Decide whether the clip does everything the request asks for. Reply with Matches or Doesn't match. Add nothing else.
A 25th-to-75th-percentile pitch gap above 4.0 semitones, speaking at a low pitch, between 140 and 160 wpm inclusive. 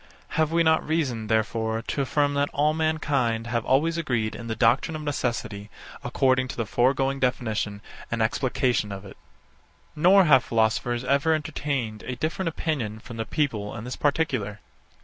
Doesn't match